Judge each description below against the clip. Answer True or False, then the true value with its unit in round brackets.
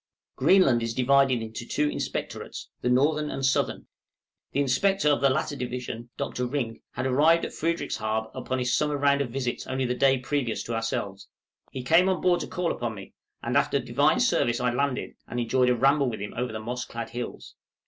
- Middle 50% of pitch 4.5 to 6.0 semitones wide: False (3.2 semitones)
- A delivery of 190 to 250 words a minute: True (200 wpm)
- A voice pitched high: False (130 Hz)